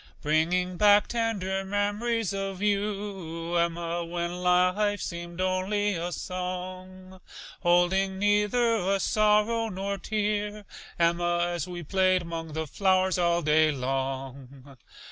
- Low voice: No, medium, 185 Hz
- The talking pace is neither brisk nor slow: No, slow, 115 wpm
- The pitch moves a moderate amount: Yes, average, 3.0 semitones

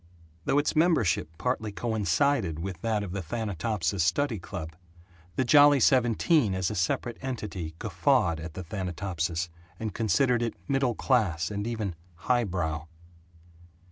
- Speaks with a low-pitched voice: Yes, low, 105 Hz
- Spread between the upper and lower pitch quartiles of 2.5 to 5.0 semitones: No, wide, 5.6 semitones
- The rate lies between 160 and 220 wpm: No, slow, 135 wpm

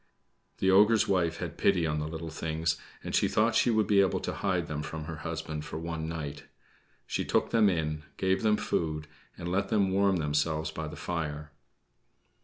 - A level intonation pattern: No, average, 3.8 semitones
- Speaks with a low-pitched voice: Yes, very low, 80 Hz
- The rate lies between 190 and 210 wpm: Yes, average, 195 wpm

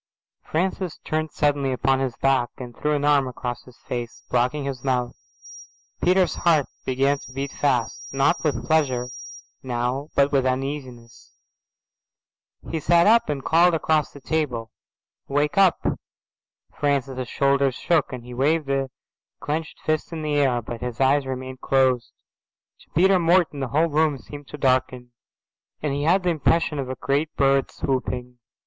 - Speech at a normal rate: Yes, average, 155 wpm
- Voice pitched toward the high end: No, medium, 140 Hz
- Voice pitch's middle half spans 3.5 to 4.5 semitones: No, average, 3.1 semitones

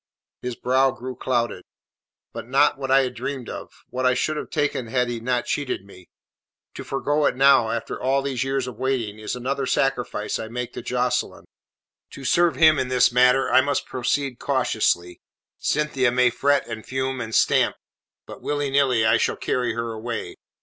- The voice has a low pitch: Yes, low, 125 Hz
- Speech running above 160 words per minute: Yes, average, 185 wpm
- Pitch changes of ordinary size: No, narrow, 2.3 semitones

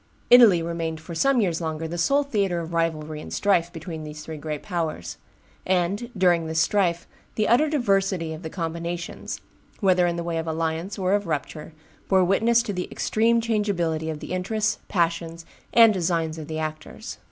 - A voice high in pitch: No, medium, 170 Hz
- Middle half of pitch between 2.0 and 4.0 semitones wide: Yes, average, 3.7 semitones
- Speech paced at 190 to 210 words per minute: No, average, 180 wpm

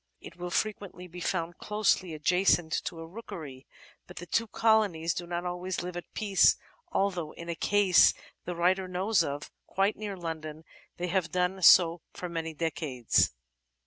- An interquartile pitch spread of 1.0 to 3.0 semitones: Yes, narrow, 2.6 semitones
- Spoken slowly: No, average, 165 wpm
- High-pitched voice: No, medium, 175 Hz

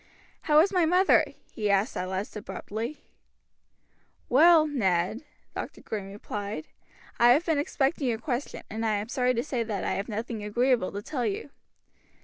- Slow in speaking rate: No, average, 165 wpm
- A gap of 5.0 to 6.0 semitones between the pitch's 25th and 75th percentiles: Yes, wide, 5.6 semitones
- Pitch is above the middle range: Yes, high, 235 Hz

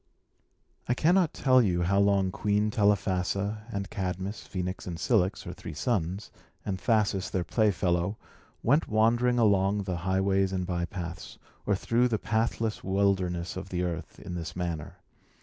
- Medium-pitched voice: No, very low, 95 Hz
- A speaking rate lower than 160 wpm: Yes, average, 150 wpm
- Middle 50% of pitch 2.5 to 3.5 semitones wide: Yes, average, 3.1 semitones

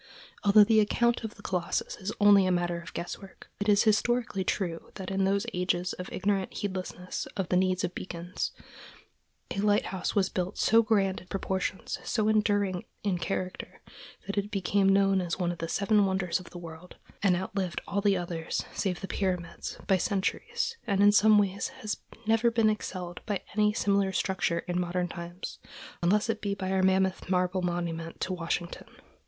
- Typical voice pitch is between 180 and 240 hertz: Yes, high, 190 Hz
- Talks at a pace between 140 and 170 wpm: No, average, 180 wpm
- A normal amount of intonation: No, narrow, 2.2 semitones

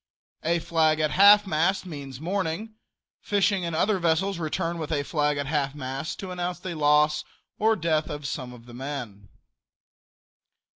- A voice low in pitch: No, medium, 160 Hz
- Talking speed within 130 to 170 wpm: Yes, average, 160 wpm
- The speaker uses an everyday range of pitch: Yes, average, 3.8 semitones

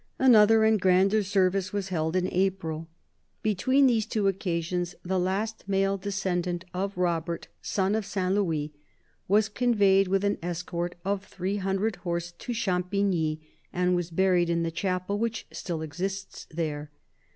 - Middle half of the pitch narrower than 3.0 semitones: Yes, narrow, 2.5 semitones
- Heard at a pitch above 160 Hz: Yes, high, 190 Hz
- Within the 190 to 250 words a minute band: No, average, 150 wpm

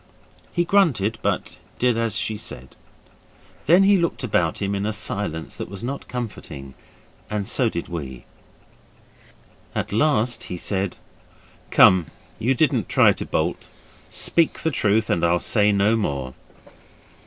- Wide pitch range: Yes, wide, 5.8 semitones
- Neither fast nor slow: Yes, average, 145 wpm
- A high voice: No, low, 105 Hz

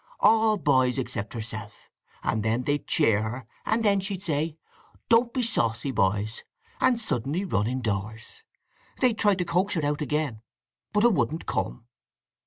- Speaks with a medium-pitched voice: Yes, medium, 145 Hz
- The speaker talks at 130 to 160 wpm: Yes, average, 155 wpm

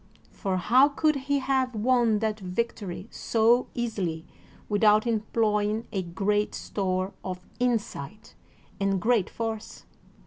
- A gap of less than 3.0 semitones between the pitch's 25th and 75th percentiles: No, average, 3.4 semitones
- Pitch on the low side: No, high, 215 Hz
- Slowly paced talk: Yes, slow, 115 wpm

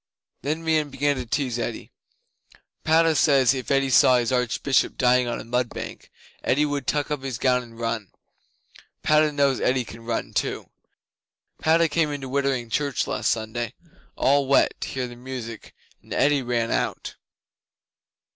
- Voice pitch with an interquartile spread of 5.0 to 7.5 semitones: No, average, 3.1 semitones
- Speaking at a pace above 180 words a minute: No, average, 160 wpm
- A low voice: Yes, low, 130 Hz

